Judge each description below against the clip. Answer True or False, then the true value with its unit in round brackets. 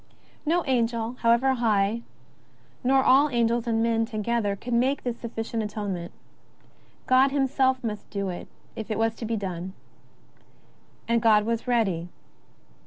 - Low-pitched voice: False (230 Hz)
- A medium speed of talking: True (150 wpm)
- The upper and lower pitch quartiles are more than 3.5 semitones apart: False (2.8 semitones)